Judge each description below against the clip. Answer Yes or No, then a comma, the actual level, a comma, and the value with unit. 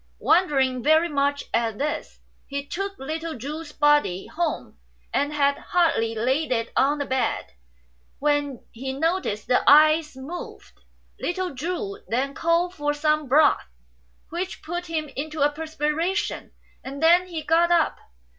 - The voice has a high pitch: Yes, very high, 300 Hz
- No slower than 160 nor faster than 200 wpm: No, average, 145 wpm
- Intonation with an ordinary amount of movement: Yes, average, 3.1 semitones